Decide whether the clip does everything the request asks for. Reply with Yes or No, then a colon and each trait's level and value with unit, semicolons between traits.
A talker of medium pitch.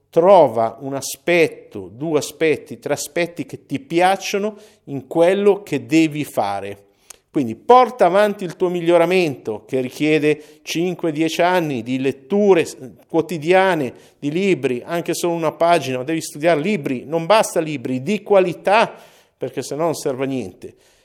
Yes: medium, 160 Hz